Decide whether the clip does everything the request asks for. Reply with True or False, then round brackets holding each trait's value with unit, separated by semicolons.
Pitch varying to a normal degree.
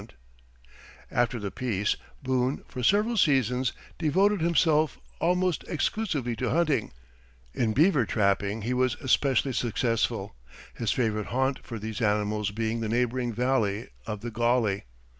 True (4.1 semitones)